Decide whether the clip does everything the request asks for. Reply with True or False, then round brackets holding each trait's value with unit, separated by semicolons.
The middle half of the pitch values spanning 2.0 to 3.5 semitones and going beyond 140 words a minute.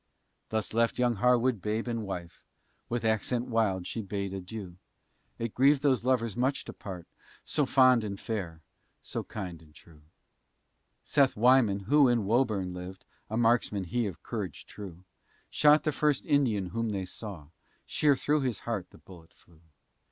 False (4.7 semitones; 160 wpm)